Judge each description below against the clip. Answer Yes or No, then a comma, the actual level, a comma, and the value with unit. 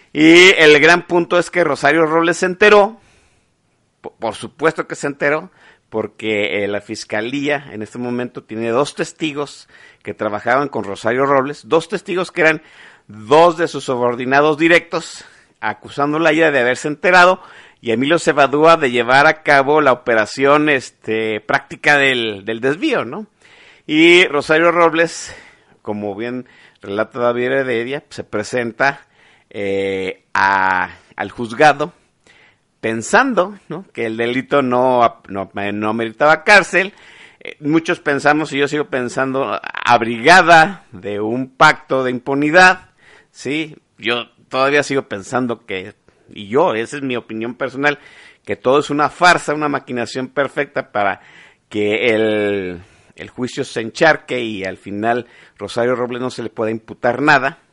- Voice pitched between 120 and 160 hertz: Yes, low, 135 Hz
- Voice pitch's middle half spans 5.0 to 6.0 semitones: Yes, wide, 5.6 semitones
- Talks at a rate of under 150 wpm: Yes, average, 140 wpm